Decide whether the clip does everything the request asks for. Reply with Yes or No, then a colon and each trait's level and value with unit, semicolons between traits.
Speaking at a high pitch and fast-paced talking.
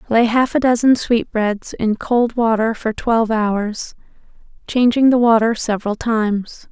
No: high, 225 Hz; average, 145 wpm